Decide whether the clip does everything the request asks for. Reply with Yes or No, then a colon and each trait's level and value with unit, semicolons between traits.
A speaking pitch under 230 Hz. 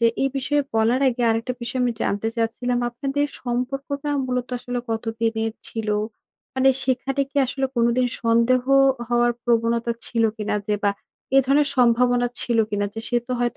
No: high, 240 Hz